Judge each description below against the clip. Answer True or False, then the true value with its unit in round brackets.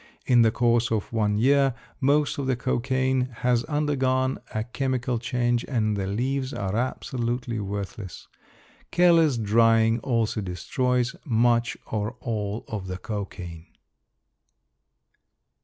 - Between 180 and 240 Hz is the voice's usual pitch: False (120 Hz)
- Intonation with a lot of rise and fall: False (3.2 semitones)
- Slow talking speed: True (120 wpm)